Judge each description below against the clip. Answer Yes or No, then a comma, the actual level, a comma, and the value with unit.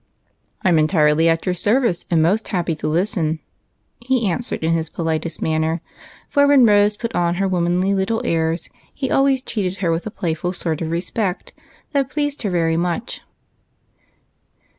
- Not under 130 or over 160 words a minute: No, average, 170 wpm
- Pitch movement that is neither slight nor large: Yes, average, 4.7 semitones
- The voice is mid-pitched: Yes, medium, 180 Hz